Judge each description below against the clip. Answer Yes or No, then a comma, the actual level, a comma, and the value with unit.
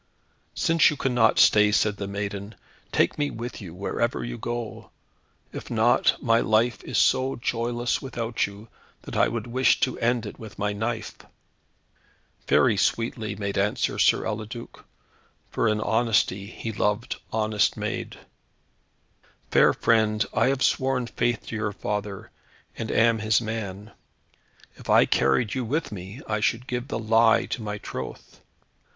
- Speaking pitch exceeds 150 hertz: No, low, 110 Hz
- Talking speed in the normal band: Yes, average, 150 wpm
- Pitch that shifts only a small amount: Yes, narrow, 2.3 semitones